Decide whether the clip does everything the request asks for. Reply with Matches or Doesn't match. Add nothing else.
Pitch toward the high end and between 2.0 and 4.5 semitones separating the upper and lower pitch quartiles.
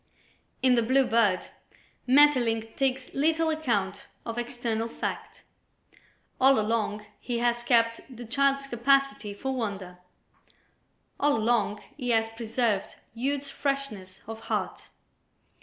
Matches